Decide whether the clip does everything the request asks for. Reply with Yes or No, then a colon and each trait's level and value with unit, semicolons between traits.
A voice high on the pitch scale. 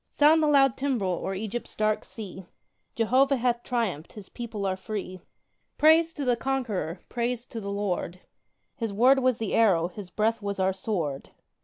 Yes: high, 220 Hz